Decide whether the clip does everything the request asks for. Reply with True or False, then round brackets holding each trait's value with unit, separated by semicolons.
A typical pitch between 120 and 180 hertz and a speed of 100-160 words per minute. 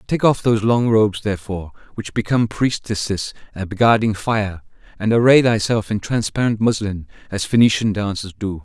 False (105 Hz; 145 wpm)